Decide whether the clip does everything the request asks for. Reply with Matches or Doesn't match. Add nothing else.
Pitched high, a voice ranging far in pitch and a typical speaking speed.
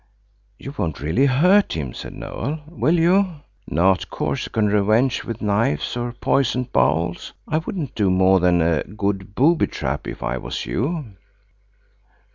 Doesn't match